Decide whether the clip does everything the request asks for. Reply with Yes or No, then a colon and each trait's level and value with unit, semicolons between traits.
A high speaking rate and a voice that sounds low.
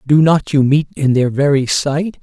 No: fast, 215 wpm; medium, 145 Hz